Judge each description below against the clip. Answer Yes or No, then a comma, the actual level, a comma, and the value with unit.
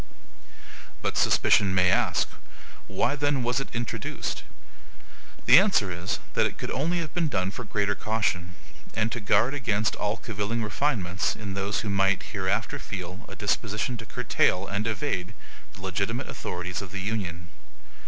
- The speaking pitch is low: Yes, low, 105 Hz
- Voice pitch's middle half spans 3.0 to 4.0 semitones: Yes, average, 3.7 semitones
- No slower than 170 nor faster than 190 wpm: No, average, 155 wpm